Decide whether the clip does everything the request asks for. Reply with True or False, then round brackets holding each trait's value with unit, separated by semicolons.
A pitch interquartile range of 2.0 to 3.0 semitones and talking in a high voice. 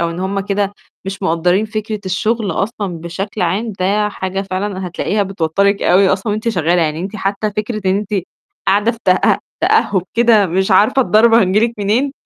True (2.4 semitones; 200 Hz)